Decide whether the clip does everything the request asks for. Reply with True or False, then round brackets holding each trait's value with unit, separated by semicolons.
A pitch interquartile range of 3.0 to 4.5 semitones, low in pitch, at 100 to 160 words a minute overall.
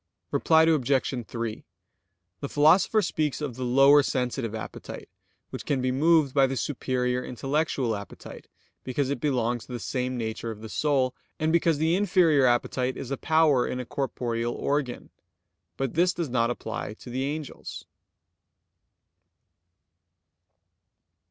True (3.6 semitones; 130 Hz; 140 wpm)